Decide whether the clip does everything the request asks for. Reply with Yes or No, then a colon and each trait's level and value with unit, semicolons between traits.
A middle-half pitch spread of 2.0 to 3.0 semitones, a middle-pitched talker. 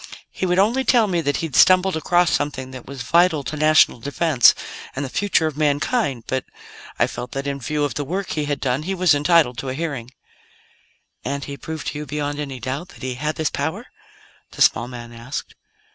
No: average, 4.1 semitones; medium, 145 Hz